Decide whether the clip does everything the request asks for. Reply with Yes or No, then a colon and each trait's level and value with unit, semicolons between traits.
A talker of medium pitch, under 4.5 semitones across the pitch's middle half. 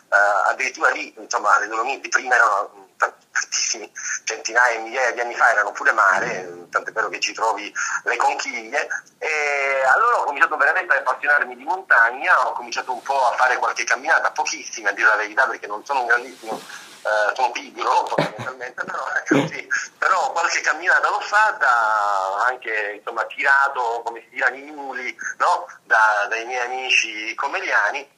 No: low, 120 Hz; average, 3.5 semitones